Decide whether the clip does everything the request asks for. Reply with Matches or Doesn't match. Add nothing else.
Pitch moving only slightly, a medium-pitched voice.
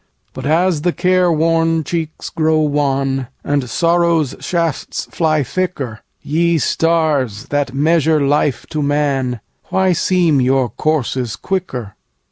Doesn't match